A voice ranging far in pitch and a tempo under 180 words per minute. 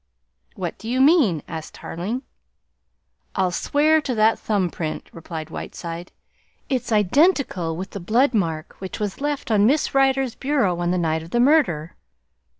Yes: wide, 7.7 semitones; average, 155 wpm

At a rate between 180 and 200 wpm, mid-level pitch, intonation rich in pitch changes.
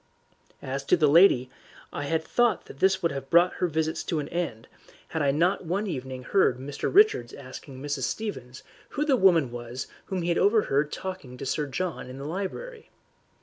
Yes: average, 190 wpm; medium, 160 Hz; wide, 5.8 semitones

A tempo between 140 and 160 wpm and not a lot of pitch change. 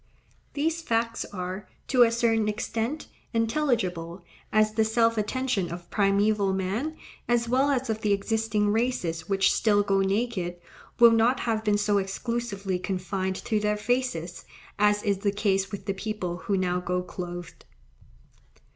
No: average, 150 wpm; average, 3.2 semitones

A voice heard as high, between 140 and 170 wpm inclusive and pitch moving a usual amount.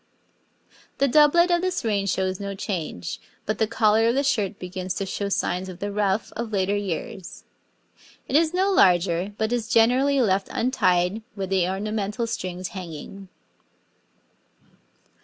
Yes: high, 205 Hz; average, 150 wpm; average, 3.8 semitones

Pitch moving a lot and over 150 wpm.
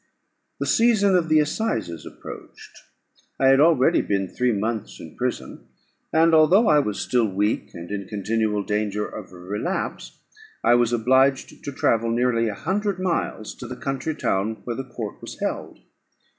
Yes: wide, 6.5 semitones; average, 165 wpm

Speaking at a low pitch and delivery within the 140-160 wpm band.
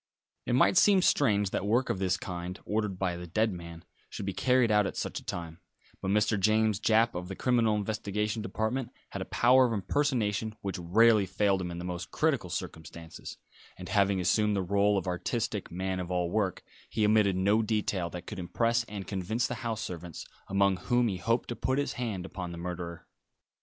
No: low, 100 Hz; average, 200 wpm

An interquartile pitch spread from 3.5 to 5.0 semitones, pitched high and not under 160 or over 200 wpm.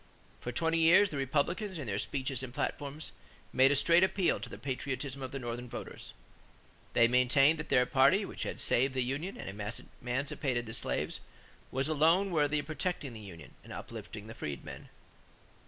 No: average, 4.2 semitones; low, 135 Hz; average, 175 wpm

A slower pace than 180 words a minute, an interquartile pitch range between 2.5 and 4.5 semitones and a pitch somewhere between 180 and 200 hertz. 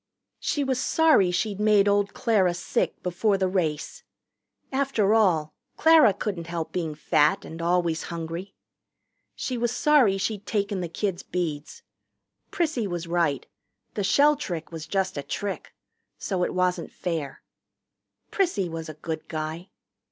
Yes: average, 145 wpm; average, 4.2 semitones; medium, 185 Hz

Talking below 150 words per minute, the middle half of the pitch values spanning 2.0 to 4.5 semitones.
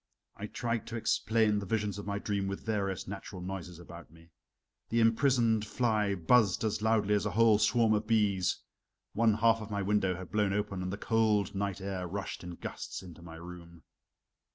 No: average, 190 wpm; average, 2.9 semitones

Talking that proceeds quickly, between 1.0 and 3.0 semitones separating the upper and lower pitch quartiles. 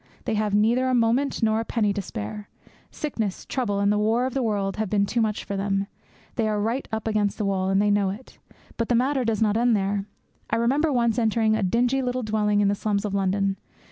Yes: fast, 235 wpm; average, 2.7 semitones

